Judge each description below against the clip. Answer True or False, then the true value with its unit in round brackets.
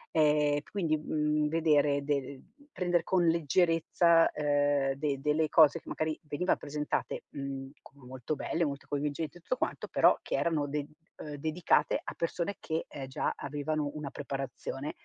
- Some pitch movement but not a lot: False (2.3 semitones)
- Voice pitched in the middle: True (150 Hz)